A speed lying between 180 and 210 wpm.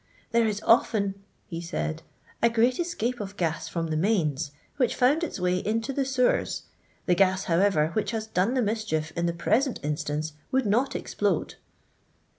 Yes: average, 185 wpm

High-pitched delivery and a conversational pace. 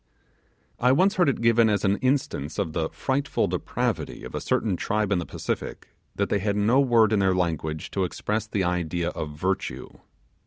No: low, 100 Hz; average, 190 wpm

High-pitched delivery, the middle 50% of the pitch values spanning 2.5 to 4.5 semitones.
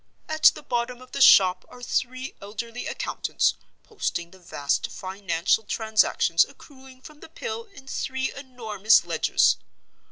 No: high, 245 Hz; average, 5.0 semitones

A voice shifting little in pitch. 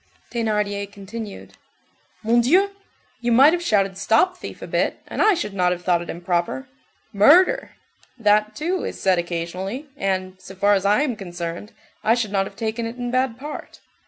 No: average, 4.4 semitones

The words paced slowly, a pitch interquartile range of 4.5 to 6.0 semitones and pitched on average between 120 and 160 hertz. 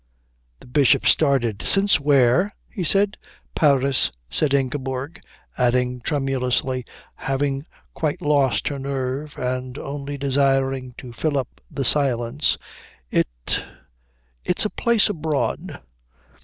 No: slow, 110 wpm; narrow, 2.5 semitones; low, 135 Hz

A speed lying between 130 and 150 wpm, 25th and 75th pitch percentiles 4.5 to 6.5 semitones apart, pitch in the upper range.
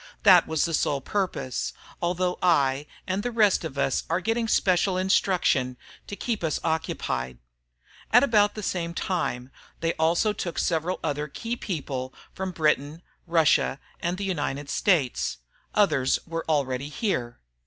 No: average, 145 wpm; average, 4.9 semitones; medium, 165 Hz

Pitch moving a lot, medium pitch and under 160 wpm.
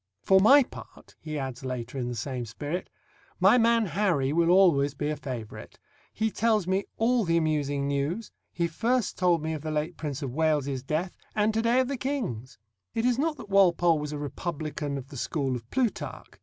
No: wide, 6.9 semitones; medium, 160 Hz; average, 200 wpm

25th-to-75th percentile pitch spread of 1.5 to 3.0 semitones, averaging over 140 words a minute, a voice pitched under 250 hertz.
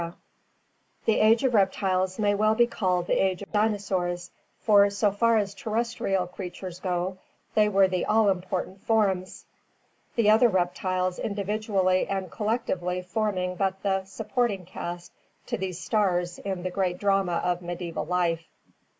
Yes: average, 2.7 semitones; average, 150 wpm; high, 190 Hz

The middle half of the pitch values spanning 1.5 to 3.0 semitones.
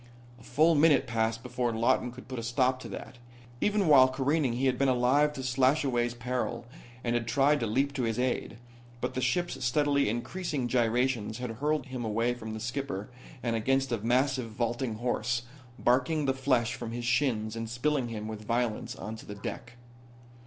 Yes: narrow, 2.5 semitones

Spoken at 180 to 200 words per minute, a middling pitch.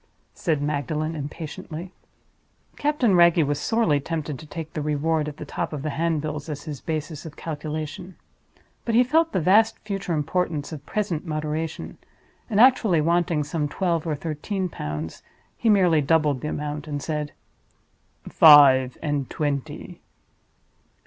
No: average, 145 wpm; medium, 155 Hz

